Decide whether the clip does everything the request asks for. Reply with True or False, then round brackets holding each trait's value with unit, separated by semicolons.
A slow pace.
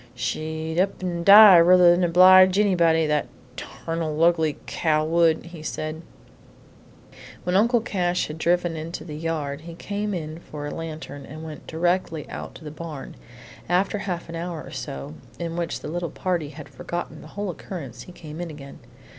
False (175 wpm)